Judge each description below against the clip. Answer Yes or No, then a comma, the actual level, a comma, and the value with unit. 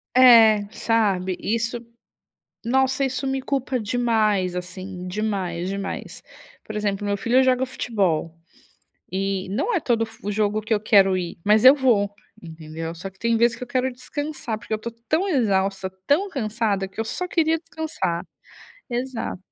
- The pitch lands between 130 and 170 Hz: No, high, 220 Hz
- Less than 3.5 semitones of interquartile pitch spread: No, average, 4.6 semitones